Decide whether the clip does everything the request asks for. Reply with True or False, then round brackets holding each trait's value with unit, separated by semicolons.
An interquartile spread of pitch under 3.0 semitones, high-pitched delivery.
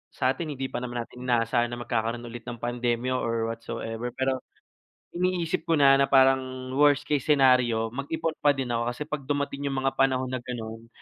False (2.6 semitones; 130 Hz)